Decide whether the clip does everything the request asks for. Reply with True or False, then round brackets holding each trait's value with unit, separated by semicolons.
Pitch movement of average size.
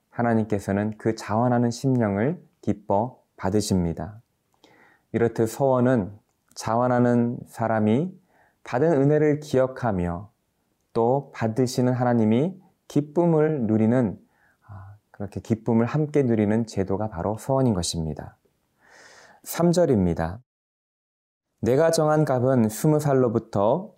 True (4.2 semitones)